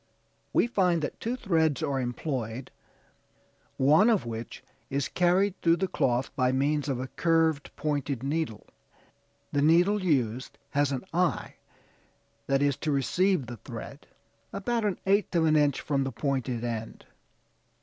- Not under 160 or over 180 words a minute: No, average, 150 wpm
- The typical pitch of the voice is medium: Yes, medium, 145 Hz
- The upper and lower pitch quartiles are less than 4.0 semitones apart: No, average, 5.0 semitones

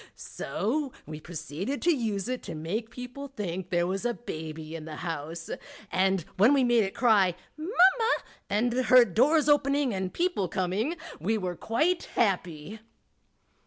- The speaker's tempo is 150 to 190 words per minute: Yes, average, 160 wpm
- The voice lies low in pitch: No, high, 215 Hz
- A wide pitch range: Yes, wide, 6.9 semitones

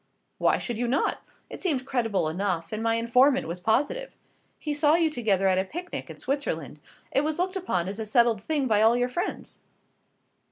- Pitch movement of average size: No, wide, 6.5 semitones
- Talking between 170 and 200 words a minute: Yes, average, 195 wpm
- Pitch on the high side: Yes, high, 240 Hz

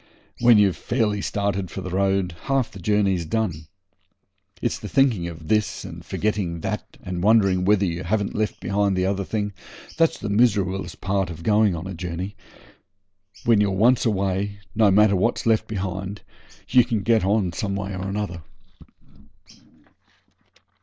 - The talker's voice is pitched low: Yes, low, 100 Hz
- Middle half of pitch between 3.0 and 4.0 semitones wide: No, narrow, 2.5 semitones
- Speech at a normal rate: Yes, average, 155 wpm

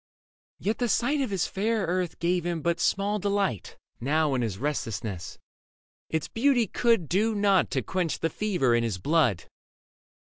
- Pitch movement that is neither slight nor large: No, wide, 6.4 semitones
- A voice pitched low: No, medium, 175 Hz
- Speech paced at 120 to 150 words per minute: No, average, 170 wpm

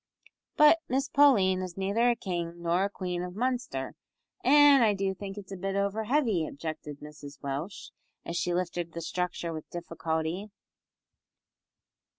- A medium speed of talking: Yes, average, 155 wpm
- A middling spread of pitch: Yes, average, 4.0 semitones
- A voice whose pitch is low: No, medium, 185 Hz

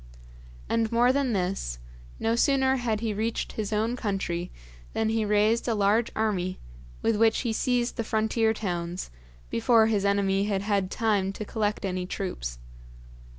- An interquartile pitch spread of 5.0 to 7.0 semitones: No, narrow, 2.6 semitones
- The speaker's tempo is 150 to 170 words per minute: Yes, average, 155 wpm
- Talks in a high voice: Yes, high, 215 Hz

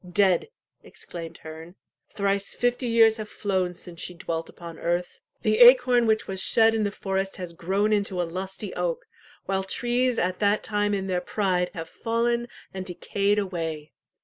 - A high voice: Yes, high, 195 Hz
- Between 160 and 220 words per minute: Yes, average, 170 wpm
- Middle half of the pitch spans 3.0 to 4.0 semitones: Yes, average, 3.4 semitones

